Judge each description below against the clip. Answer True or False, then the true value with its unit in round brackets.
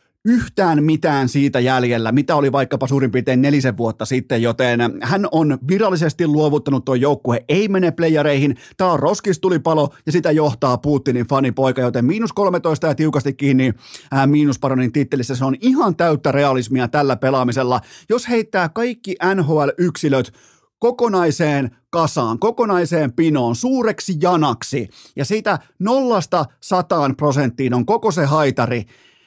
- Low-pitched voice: False (145 Hz)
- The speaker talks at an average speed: True (135 wpm)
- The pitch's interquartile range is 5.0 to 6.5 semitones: True (5.3 semitones)